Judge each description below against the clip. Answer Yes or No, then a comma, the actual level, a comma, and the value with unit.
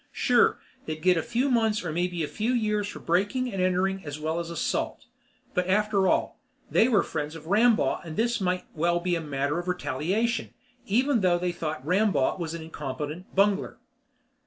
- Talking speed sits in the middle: Yes, average, 185 wpm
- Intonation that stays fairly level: No, average, 4.6 semitones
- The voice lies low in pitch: No, medium, 180 Hz